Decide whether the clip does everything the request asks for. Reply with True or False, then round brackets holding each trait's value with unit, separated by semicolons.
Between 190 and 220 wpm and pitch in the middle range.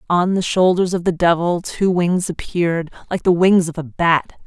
True (200 wpm; 175 Hz)